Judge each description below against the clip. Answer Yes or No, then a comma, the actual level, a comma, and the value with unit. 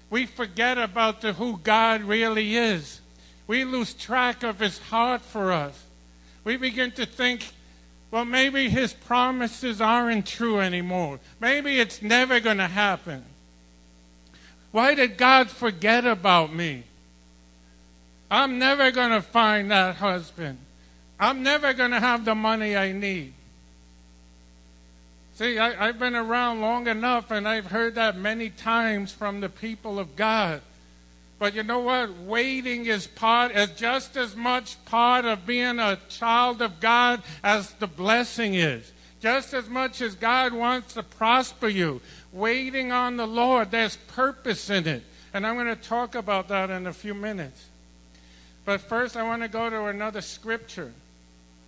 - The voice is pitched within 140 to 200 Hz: No, high, 220 Hz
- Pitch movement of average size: No, wide, 6.0 semitones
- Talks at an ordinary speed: Yes, average, 155 wpm